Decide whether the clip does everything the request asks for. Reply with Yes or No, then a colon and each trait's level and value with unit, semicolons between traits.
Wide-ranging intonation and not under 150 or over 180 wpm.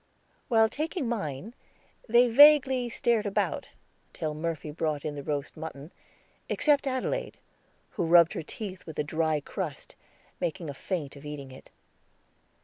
No: wide, 8.0 semitones; average, 140 wpm